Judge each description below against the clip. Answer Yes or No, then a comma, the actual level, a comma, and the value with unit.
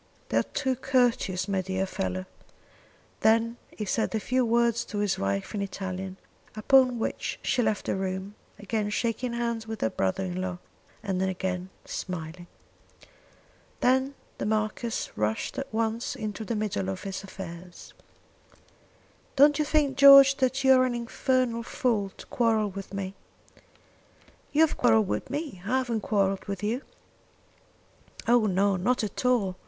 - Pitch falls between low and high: No, high, 215 Hz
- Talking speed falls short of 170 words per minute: Yes, average, 155 wpm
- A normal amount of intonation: Yes, average, 4.5 semitones